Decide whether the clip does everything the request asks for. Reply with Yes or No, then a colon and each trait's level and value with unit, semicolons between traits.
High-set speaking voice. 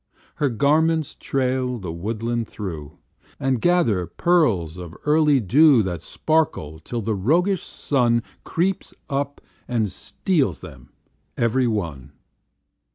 No: low, 120 Hz